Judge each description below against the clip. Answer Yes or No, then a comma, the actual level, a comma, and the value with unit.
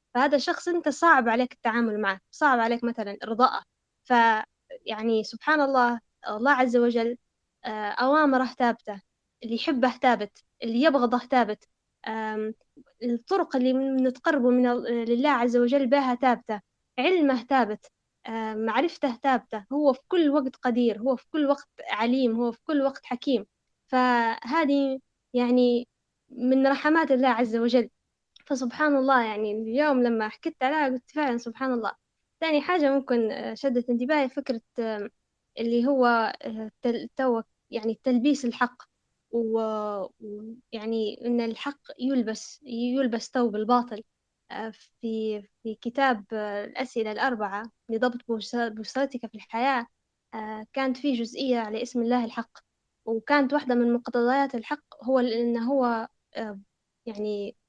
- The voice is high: Yes, high, 245 Hz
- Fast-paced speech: No, average, 120 wpm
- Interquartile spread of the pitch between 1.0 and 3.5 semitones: Yes, average, 3.0 semitones